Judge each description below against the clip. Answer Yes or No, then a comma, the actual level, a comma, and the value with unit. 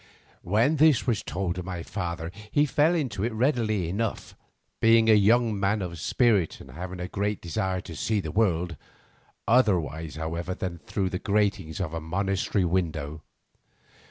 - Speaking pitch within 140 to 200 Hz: No, very low, 95 Hz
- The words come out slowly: No, average, 160 wpm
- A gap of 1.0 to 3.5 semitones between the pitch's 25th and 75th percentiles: No, average, 4.4 semitones